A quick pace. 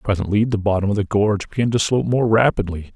Yes: fast, 225 wpm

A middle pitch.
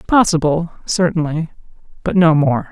Yes: medium, 165 Hz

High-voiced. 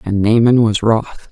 No: low, 110 Hz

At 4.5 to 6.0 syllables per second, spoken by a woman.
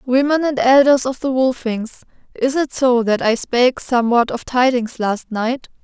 Yes: 4.6 syllables/s; female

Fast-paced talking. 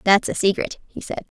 Yes: fast, 215 wpm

